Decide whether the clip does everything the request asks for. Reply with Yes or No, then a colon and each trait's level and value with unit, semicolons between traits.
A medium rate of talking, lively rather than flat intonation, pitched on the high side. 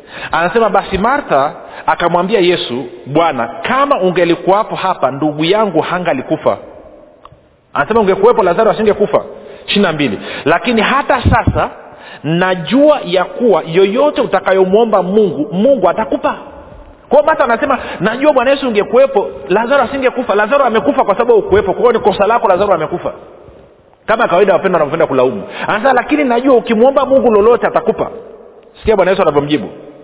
Yes: average, 130 wpm; wide, 7.0 semitones; high, 215 Hz